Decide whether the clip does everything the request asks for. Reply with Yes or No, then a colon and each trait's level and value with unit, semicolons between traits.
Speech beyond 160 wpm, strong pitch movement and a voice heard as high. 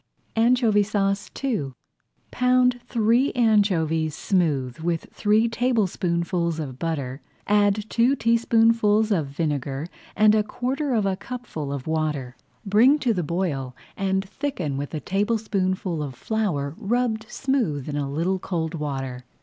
No: slow, 135 wpm; wide, 6.7 semitones; high, 195 Hz